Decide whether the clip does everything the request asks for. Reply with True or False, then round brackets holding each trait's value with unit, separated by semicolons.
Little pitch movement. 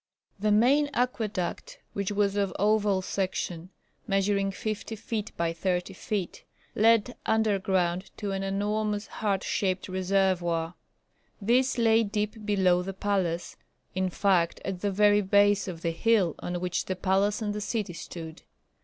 True (2.2 semitones)